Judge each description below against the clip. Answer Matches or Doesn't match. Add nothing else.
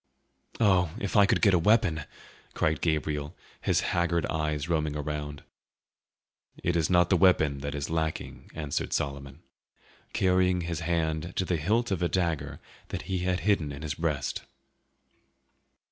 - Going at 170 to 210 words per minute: Doesn't match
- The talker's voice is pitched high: Doesn't match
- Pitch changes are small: Doesn't match